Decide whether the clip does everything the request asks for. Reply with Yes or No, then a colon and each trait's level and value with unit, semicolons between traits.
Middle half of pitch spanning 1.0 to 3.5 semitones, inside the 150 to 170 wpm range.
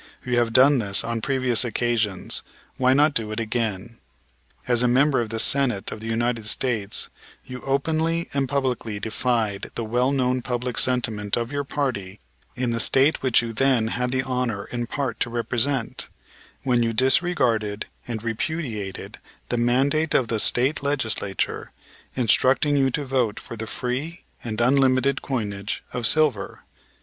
Yes: average, 3.0 semitones; average, 160 wpm